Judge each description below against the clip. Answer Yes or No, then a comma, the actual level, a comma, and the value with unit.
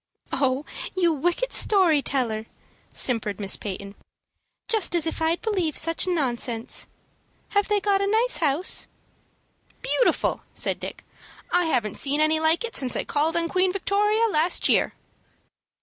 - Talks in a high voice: Yes, very high, 330 Hz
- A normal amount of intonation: No, wide, 6.5 semitones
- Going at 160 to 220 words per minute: No, average, 145 wpm